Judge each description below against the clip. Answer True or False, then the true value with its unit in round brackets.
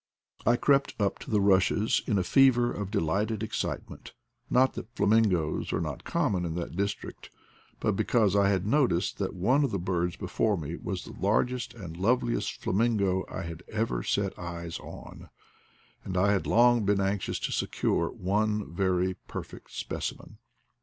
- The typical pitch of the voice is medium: False (100 Hz)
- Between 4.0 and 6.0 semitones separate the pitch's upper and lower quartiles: False (3.5 semitones)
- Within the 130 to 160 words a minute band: False (170 wpm)